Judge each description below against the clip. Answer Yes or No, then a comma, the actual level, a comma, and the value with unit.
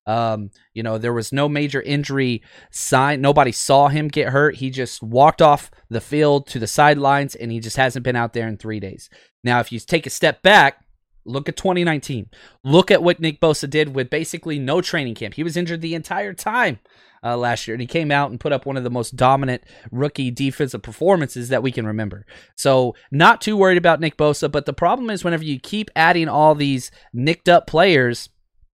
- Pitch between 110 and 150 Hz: Yes, medium, 140 Hz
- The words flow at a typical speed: No, fast, 215 wpm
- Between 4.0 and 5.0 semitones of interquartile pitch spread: Yes, average, 4.3 semitones